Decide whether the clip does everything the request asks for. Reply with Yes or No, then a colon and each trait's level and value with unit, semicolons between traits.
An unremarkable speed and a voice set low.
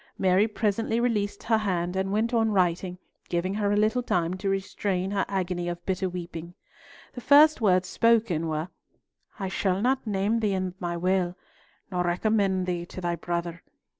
No: average, 170 wpm; high, 190 Hz